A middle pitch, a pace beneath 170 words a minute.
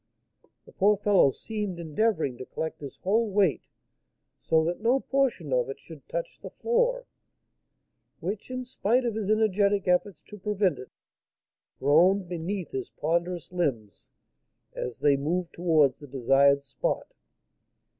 Yes: medium, 180 Hz; average, 140 wpm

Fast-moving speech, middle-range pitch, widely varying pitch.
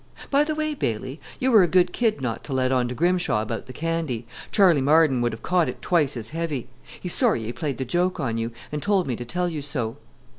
Yes: fast, 245 wpm; medium, 150 Hz; wide, 6.5 semitones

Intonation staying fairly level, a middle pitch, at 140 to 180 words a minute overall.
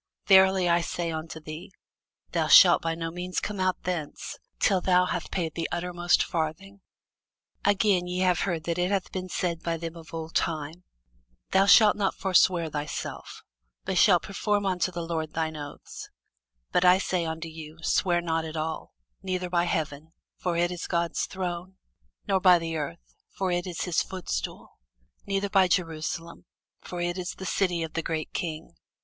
Yes: narrow, 2.2 semitones; medium, 175 Hz; average, 175 wpm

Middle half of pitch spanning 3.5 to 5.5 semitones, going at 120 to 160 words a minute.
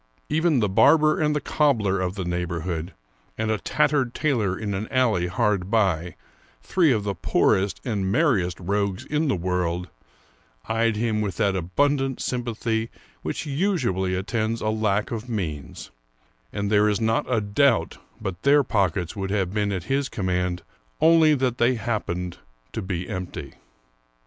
Yes: average, 5.1 semitones; average, 155 wpm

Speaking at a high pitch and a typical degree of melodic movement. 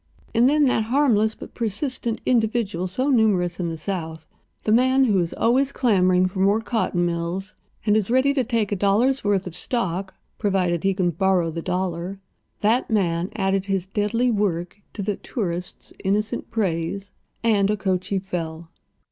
Yes: high, 200 Hz; average, 3.9 semitones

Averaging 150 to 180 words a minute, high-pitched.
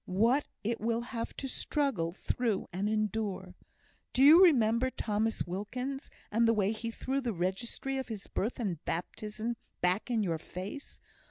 Yes: average, 160 wpm; high, 225 Hz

